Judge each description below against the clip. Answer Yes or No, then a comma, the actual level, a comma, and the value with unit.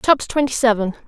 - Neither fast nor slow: Yes, average, 170 wpm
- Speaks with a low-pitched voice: No, high, 245 Hz